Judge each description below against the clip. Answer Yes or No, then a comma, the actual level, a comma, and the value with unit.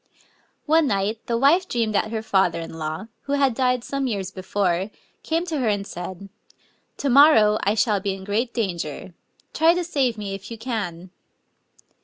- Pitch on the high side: Yes, high, 215 Hz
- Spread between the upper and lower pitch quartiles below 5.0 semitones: No, wide, 5.5 semitones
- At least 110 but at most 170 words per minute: No, average, 185 wpm